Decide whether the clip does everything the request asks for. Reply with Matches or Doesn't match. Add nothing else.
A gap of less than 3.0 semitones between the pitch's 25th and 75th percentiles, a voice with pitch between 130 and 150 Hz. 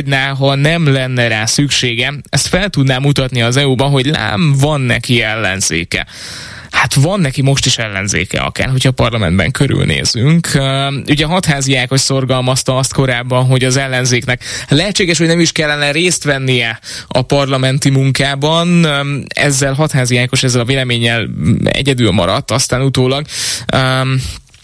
Matches